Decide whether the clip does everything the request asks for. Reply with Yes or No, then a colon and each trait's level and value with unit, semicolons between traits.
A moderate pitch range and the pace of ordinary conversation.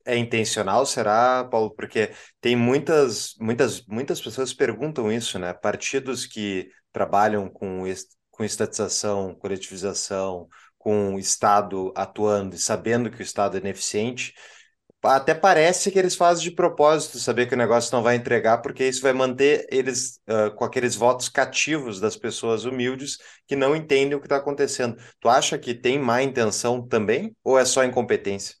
Yes: average, 4.3 semitones; average, 165 wpm